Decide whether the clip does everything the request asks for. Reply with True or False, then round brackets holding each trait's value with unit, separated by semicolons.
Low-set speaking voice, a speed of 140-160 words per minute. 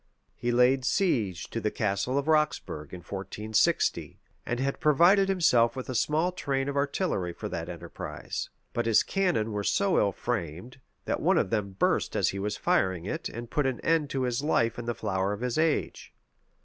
False (120 Hz; 190 wpm)